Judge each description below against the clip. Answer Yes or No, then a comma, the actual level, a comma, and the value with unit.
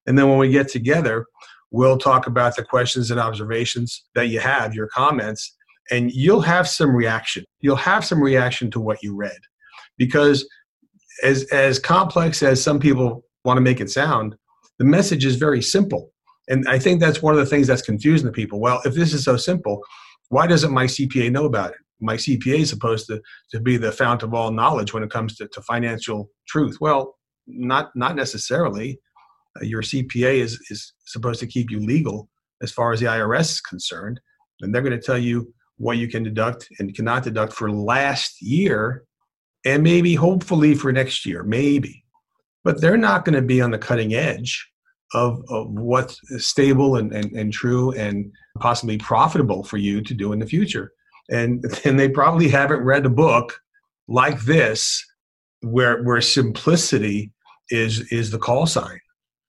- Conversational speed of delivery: Yes, average, 185 wpm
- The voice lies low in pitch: Yes, low, 125 Hz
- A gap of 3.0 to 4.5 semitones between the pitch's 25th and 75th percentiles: Yes, average, 4.1 semitones